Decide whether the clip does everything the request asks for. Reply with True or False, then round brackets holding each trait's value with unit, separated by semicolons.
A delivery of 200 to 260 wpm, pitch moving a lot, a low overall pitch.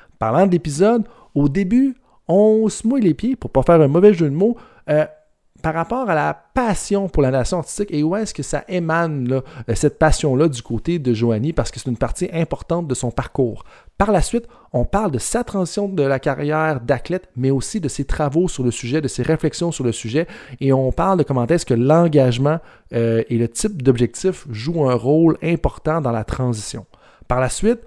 False (215 wpm; 5.8 semitones; 155 Hz)